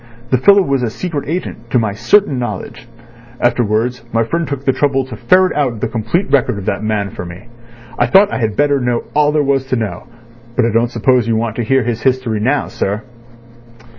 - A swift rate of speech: Yes, fast, 215 wpm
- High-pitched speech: No, low, 125 Hz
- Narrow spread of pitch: No, average, 3.9 semitones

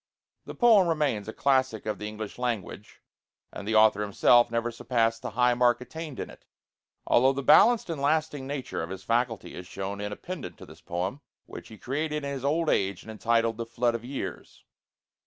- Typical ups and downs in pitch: Yes, average, 4.6 semitones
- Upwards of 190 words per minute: Yes, average, 200 wpm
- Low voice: Yes, low, 120 Hz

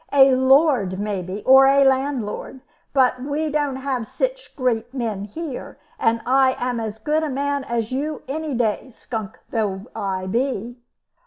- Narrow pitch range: No, average, 4.0 semitones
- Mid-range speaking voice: No, very high, 255 Hz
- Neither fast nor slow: Yes, average, 155 wpm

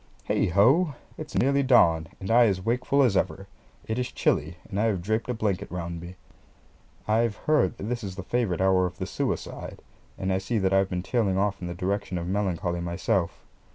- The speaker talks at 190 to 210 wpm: Yes, fast, 205 wpm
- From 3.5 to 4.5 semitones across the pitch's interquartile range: Yes, average, 4.2 semitones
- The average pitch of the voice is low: Yes, very low, 95 Hz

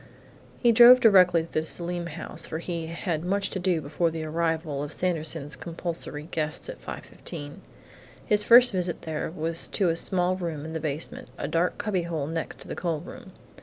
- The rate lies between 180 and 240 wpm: Yes, average, 185 wpm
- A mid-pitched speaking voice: Yes, medium, 170 Hz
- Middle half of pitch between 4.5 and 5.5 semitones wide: No, narrow, 2.4 semitones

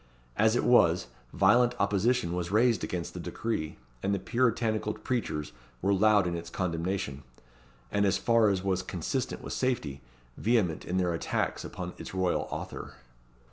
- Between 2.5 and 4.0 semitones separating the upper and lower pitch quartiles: No, average, 4.6 semitones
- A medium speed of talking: Yes, average, 155 wpm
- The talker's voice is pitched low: Yes, low, 100 Hz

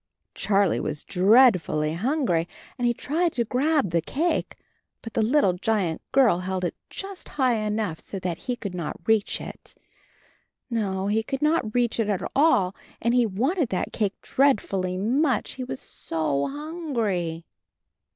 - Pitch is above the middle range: Yes, high, 220 Hz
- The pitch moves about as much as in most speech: No, wide, 6.5 semitones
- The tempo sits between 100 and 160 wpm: Yes, average, 155 wpm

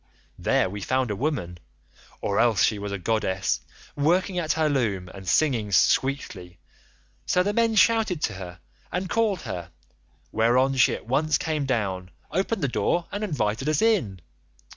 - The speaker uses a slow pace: No, average, 165 wpm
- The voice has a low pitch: Yes, low, 130 Hz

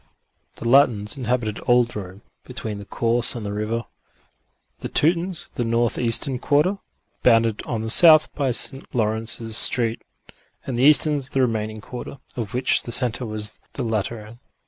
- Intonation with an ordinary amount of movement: Yes, average, 3.0 semitones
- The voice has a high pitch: No, low, 120 Hz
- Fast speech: No, average, 150 wpm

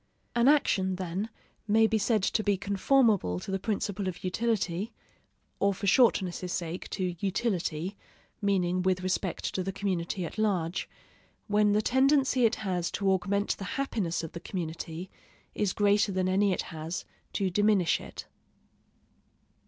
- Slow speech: No, average, 150 wpm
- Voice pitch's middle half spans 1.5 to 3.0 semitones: Yes, average, 2.7 semitones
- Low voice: No, high, 195 Hz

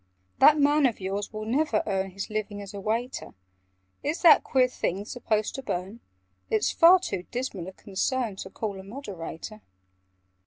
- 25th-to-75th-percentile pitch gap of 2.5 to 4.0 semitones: No, average, 4.9 semitones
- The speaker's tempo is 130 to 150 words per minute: No, average, 165 wpm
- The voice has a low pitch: No, high, 215 Hz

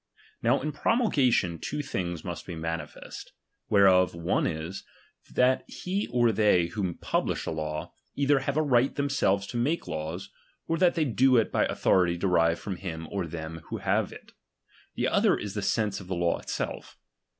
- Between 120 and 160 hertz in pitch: No, low, 100 Hz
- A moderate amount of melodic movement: No, wide, 7.5 semitones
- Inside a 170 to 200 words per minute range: Yes, average, 180 wpm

